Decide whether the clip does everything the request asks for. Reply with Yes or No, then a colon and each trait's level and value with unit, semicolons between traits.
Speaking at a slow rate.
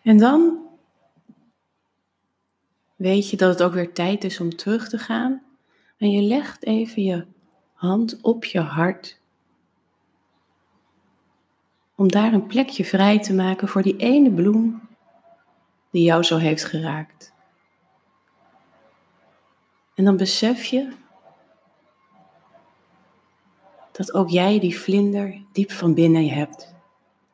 Yes: slow, 115 wpm